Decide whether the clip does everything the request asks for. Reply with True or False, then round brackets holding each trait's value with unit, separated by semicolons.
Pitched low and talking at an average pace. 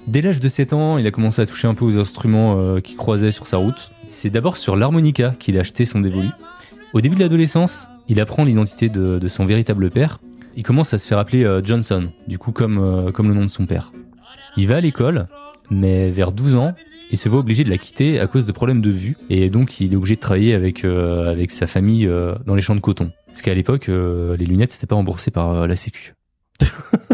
False (110 Hz; 245 wpm)